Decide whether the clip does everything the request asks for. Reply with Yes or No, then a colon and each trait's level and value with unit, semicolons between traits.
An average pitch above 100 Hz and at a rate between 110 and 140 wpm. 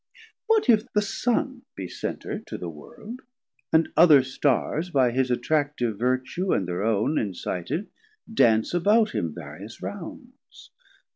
Yes: medium, 140 Hz; slow, 135 wpm